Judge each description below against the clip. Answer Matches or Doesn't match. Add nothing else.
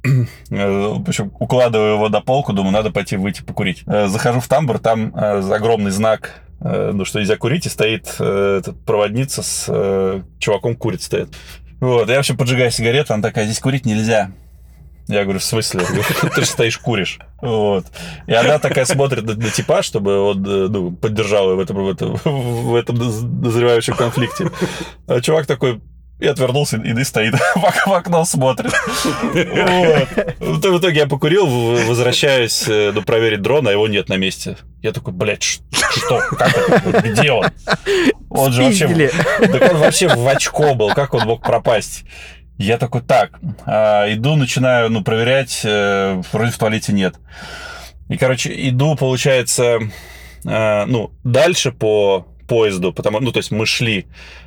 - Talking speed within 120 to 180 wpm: Matches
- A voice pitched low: Matches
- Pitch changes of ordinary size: Matches